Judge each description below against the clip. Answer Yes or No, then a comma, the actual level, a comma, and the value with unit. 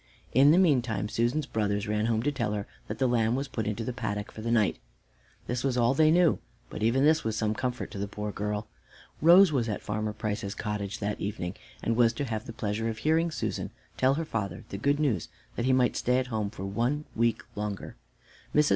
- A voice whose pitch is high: No, low, 115 Hz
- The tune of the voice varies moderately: Yes, average, 4.0 semitones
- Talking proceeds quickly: Yes, fast, 225 wpm